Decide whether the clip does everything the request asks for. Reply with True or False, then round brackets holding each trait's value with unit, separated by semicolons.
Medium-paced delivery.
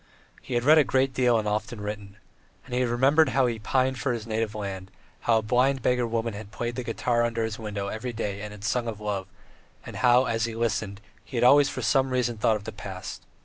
False (235 wpm)